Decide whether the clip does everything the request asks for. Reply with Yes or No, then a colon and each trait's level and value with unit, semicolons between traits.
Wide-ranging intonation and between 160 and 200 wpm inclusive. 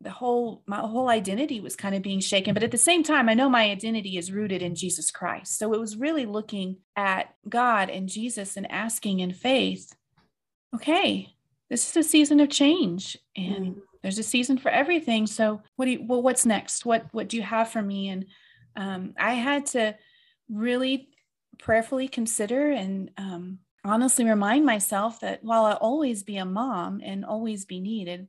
No: average, 4.2 semitones; average, 185 wpm